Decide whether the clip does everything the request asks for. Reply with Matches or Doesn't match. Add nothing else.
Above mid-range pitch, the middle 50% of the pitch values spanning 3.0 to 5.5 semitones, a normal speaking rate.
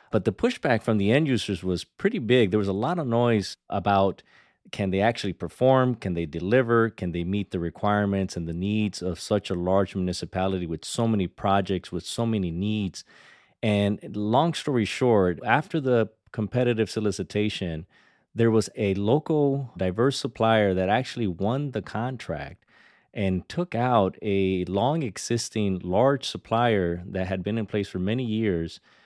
Doesn't match